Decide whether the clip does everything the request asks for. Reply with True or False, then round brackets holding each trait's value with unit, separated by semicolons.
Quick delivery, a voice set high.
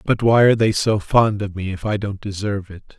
False (260 wpm; 105 Hz)